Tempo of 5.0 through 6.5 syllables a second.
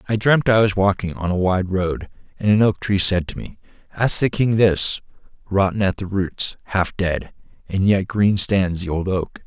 No: 4.5 syllables/s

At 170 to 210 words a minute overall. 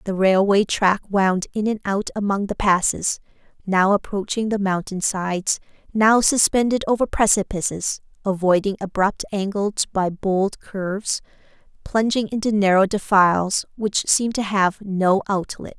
No: slow, 135 wpm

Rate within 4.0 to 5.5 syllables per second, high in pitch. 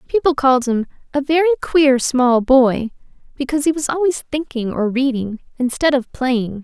Yes: 5.0 syllables/s; very high, 265 Hz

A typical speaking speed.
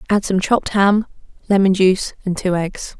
Yes: average, 180 wpm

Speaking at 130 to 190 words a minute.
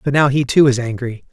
No: fast, 275 wpm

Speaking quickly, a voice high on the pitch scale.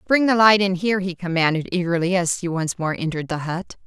No: fast, 235 wpm; medium, 180 Hz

